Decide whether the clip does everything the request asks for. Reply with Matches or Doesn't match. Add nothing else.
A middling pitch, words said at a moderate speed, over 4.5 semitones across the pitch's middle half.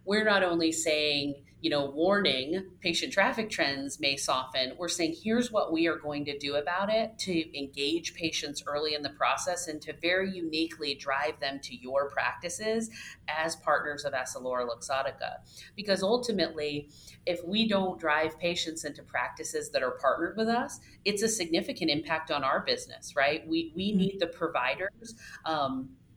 Matches